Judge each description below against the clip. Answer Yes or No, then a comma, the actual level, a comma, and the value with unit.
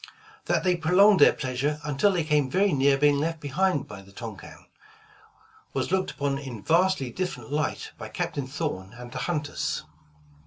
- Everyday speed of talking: Yes, average, 165 wpm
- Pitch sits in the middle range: Yes, medium, 145 Hz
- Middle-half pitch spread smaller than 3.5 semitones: No, average, 5.0 semitones